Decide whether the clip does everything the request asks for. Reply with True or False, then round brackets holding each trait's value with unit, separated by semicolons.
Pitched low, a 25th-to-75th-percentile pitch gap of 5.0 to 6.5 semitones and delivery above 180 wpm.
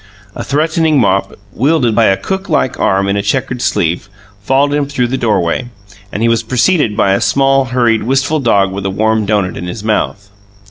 True (115 Hz; 5.4 semitones; 190 wpm)